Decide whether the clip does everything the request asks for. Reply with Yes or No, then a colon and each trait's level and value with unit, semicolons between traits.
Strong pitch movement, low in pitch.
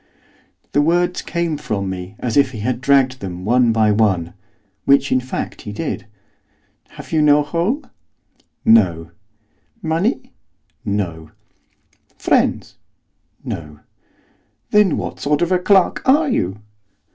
Yes: wide, 8.3 semitones; low, 130 Hz